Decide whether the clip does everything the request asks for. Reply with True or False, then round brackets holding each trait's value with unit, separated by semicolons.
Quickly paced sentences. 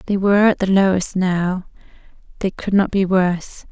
False (180 wpm)